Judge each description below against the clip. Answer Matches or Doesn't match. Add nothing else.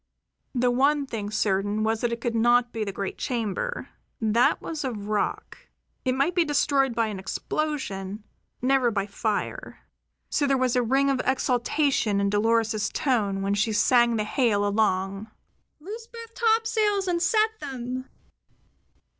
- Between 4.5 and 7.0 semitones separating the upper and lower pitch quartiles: Matches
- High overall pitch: Matches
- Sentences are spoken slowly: Doesn't match